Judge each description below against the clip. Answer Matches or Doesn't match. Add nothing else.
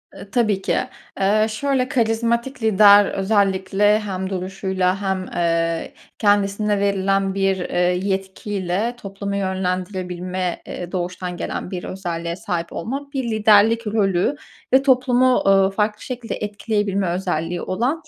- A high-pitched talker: Matches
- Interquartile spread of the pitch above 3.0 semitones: Doesn't match